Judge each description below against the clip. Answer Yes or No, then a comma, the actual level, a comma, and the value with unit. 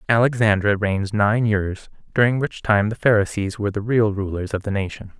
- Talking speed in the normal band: Yes, average, 185 wpm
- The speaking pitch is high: No, low, 105 Hz